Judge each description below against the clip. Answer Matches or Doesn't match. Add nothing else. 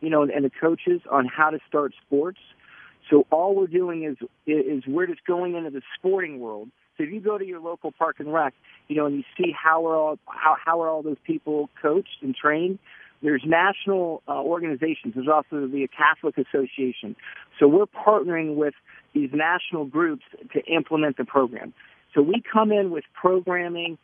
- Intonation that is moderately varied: Matches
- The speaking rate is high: Doesn't match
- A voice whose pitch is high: Doesn't match